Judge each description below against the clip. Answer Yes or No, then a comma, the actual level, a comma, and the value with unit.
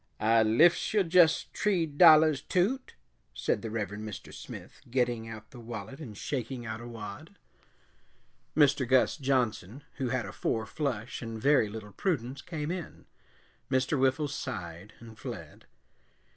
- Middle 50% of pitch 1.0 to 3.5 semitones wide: No, average, 5.1 semitones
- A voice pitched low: Yes, low, 130 Hz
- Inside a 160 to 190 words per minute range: No, average, 145 wpm